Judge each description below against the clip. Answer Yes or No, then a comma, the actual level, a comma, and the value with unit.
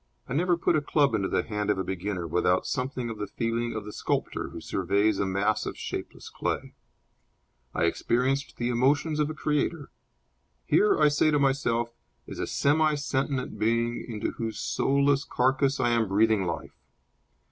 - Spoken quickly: No, average, 175 wpm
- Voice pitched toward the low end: Yes, low, 120 Hz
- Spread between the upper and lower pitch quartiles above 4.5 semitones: Yes, average, 5.2 semitones